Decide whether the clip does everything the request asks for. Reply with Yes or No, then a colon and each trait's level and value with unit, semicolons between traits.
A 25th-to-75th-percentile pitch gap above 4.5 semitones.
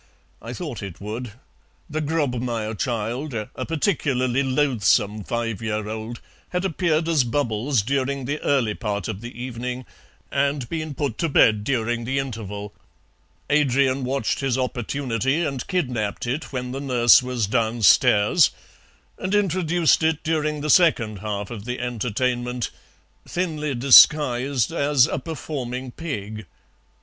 No: average, 4.2 semitones